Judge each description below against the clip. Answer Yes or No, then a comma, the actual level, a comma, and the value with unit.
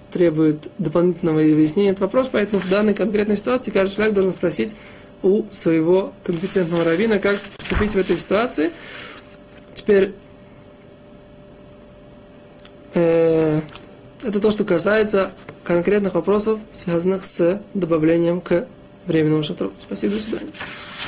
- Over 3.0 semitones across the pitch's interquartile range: Yes, average, 3.4 semitones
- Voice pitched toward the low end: No, high, 190 Hz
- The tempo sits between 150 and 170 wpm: No, average, 115 wpm